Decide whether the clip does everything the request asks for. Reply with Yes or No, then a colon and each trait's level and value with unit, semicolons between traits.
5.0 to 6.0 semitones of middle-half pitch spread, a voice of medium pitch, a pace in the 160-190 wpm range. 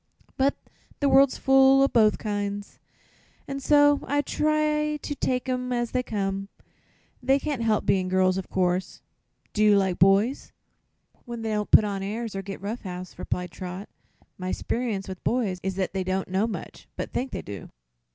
No: wide, 5.5 semitones; high, 215 Hz; average, 180 wpm